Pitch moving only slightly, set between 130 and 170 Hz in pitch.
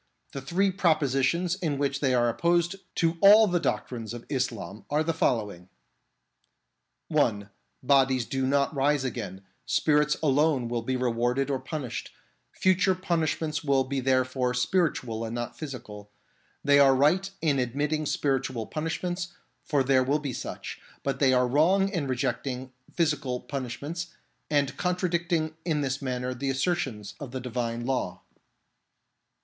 No: average, 4.0 semitones; low, 135 Hz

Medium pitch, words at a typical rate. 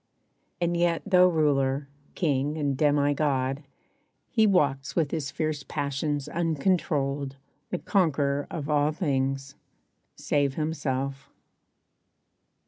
No: medium, 145 Hz; slow, 105 wpm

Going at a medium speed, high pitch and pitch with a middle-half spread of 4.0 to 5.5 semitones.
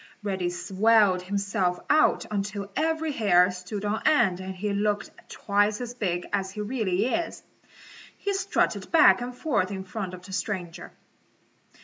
No: average, 150 wpm; high, 200 Hz; average, 3.3 semitones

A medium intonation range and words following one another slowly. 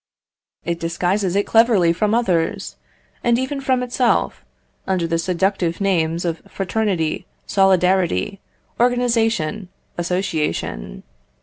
Yes: average, 4.8 semitones; slow, 100 wpm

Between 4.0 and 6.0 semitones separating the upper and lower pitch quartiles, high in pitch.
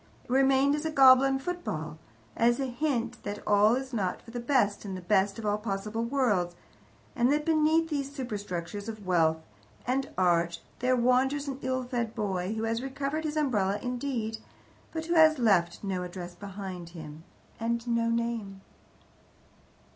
Yes: wide, 5.4 semitones; high, 230 Hz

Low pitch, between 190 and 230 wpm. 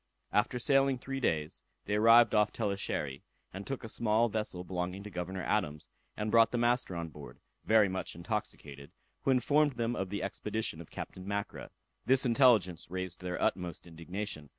No: low, 100 Hz; average, 170 wpm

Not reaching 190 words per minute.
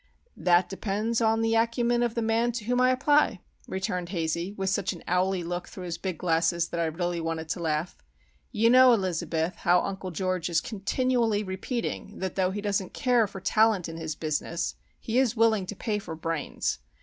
No: average, 195 wpm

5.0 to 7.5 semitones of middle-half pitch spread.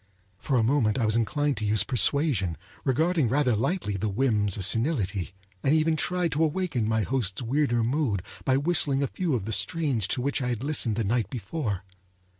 Yes: wide, 5.4 semitones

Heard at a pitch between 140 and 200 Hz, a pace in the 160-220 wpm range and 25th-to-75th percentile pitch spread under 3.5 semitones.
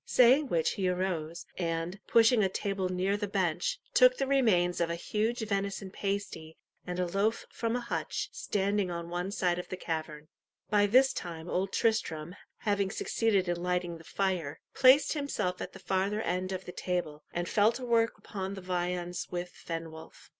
Yes: medium, 185 Hz; average, 180 wpm; average, 3.1 semitones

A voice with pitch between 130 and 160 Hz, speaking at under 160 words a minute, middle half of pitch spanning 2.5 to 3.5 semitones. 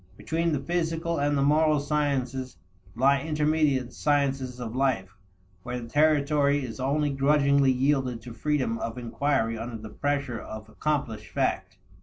Yes: medium, 140 Hz; average, 145 wpm; average, 3.2 semitones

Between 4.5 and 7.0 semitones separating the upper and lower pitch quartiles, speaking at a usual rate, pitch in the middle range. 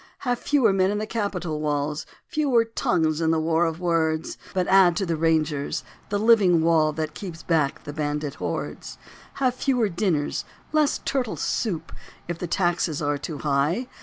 Yes: average, 5.0 semitones; average, 170 wpm; medium, 170 Hz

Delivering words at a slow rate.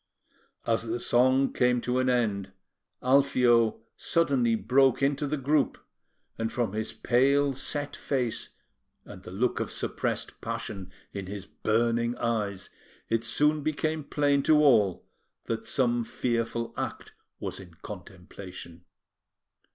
Yes: slow, 130 wpm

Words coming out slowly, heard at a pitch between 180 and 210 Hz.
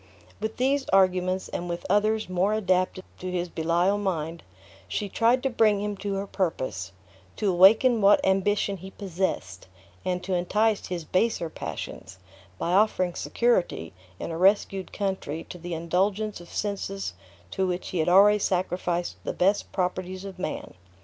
No: average, 155 wpm; high, 190 Hz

